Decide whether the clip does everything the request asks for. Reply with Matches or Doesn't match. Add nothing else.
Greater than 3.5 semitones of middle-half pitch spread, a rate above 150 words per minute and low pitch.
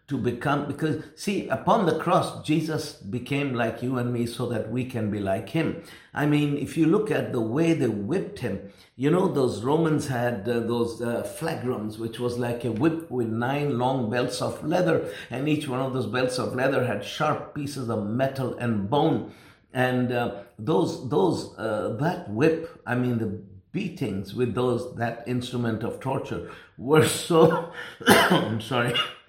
Matches